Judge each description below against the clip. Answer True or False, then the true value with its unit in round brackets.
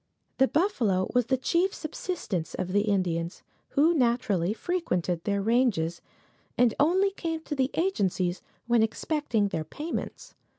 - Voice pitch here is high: True (235 Hz)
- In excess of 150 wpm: False (135 wpm)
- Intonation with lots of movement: True (9.0 semitones)